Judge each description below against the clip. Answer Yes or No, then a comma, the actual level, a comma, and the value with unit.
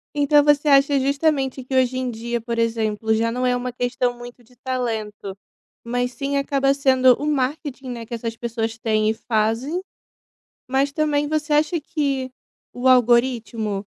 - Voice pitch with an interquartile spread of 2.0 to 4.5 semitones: Yes, average, 3.2 semitones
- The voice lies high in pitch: Yes, very high, 255 Hz